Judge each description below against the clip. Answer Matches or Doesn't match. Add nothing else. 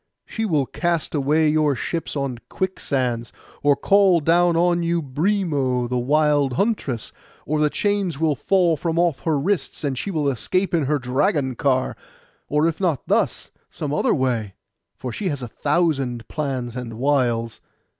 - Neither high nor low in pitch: Matches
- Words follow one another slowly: Doesn't match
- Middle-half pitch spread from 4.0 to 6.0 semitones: Matches